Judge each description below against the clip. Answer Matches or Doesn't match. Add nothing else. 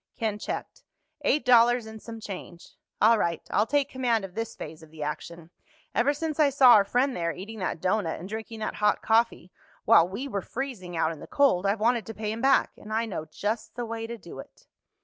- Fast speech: Matches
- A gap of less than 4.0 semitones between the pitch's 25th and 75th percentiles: Doesn't match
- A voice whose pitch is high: Matches